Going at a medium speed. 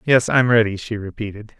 Yes: average, 190 wpm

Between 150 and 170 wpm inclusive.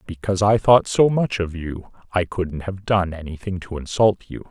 No: average, 200 wpm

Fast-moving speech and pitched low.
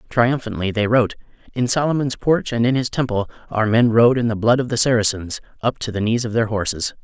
Yes: fast, 220 wpm; low, 115 Hz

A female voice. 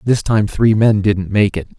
No: male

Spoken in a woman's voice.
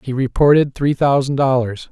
No: male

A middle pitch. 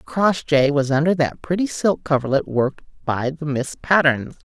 Yes: medium, 150 Hz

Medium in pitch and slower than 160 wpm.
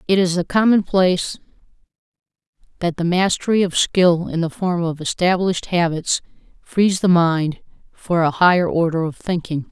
Yes: medium, 175 Hz; average, 150 wpm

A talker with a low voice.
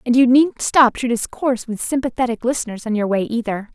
No: high, 240 Hz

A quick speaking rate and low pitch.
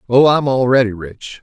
No: average, 170 wpm; low, 125 Hz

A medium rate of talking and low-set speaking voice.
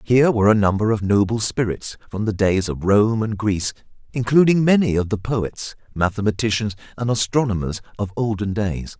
Yes: average, 165 wpm; low, 105 Hz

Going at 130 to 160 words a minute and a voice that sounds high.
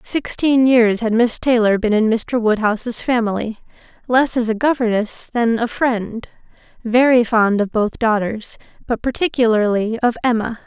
Yes: average, 145 wpm; high, 230 Hz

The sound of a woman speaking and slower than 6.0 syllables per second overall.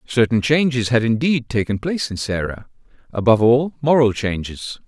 No: male; 5.2 syllables/s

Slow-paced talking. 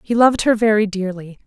No: fast, 205 wpm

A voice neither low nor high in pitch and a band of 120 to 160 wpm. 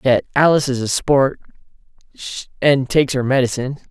No: low, 130 Hz; average, 140 wpm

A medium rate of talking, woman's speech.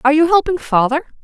Yes: average, 195 wpm; female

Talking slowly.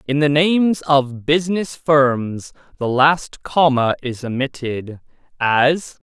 Yes: slow, 120 wpm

